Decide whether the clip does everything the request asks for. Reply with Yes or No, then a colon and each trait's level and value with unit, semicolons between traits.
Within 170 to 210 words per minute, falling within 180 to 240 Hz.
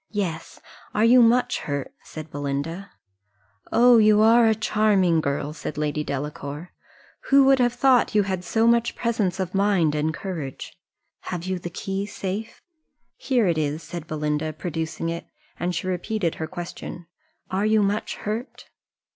No: average, 155 wpm; medium, 185 Hz